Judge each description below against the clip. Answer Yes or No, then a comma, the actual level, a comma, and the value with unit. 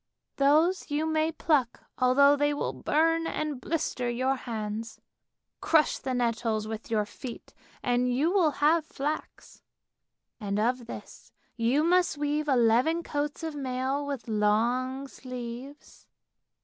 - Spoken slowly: Yes, slow, 130 wpm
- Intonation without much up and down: No, average, 4.1 semitones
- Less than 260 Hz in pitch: No, very high, 270 Hz